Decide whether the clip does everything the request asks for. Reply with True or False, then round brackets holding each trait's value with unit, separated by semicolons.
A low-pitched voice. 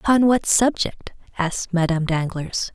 False (190 Hz)